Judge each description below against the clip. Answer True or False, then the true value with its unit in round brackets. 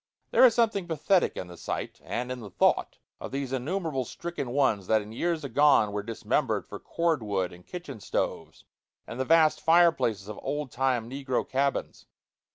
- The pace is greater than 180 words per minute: False (175 wpm)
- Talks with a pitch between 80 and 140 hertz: True (135 Hz)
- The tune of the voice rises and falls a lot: True (6.6 semitones)